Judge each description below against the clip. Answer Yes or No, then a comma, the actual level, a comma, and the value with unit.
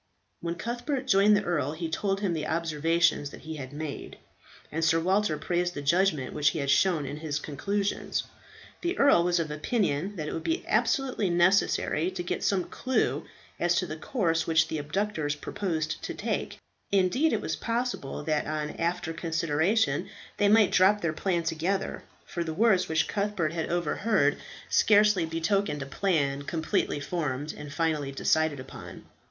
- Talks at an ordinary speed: Yes, average, 170 wpm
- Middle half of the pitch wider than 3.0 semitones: Yes, average, 4.4 semitones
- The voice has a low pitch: No, medium, 170 Hz